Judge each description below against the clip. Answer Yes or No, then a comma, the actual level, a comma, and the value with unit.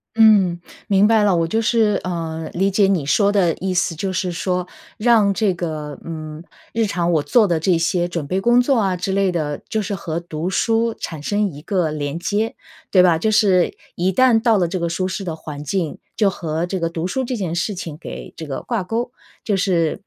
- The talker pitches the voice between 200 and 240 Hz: No, medium, 185 Hz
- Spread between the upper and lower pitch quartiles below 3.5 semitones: No, average, 3.8 semitones